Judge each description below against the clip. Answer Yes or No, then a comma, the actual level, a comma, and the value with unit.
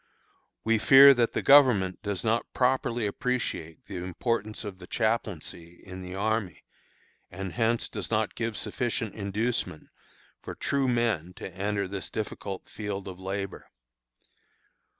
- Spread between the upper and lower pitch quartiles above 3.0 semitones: Yes, average, 3.6 semitones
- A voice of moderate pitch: No, low, 105 Hz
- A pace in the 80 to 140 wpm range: Yes, slow, 135 wpm